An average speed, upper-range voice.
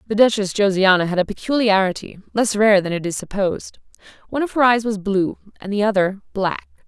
Yes: average, 190 wpm; high, 205 Hz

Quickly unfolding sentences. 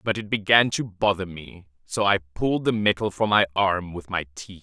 Yes: fast, 220 wpm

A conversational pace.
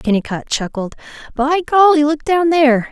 Yes: average, 145 wpm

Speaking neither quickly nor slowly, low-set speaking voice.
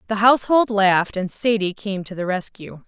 No: average, 190 wpm; high, 205 Hz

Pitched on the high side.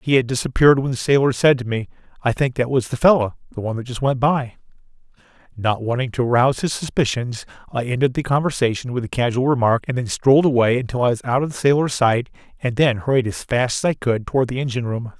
No: low, 125 Hz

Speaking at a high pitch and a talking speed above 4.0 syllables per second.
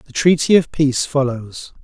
No: medium, 140 Hz; 5.0 syllables/s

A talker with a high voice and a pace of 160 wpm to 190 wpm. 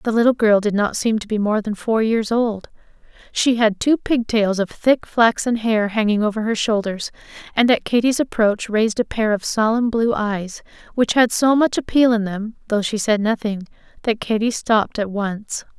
No: high, 220 Hz; average, 200 wpm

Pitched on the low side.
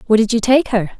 No: high, 225 Hz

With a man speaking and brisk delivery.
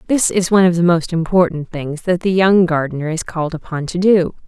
No: female; fast, 230 wpm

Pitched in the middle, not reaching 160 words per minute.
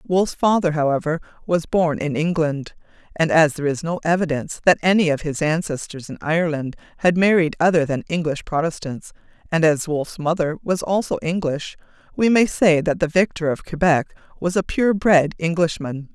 No: medium, 165 Hz; average, 170 wpm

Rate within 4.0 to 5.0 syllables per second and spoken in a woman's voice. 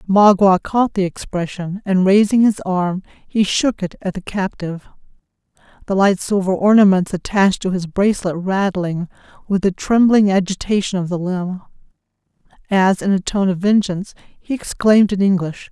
Yes: 4.9 syllables/s; female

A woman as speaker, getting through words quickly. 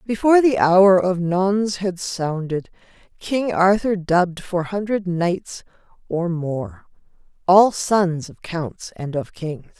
No: female; slow, 135 wpm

